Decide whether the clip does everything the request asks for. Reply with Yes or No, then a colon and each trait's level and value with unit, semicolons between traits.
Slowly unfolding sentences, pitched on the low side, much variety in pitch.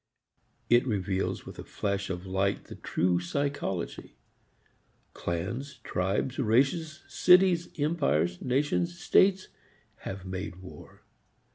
Yes: slow, 105 wpm; low, 110 Hz; wide, 7.6 semitones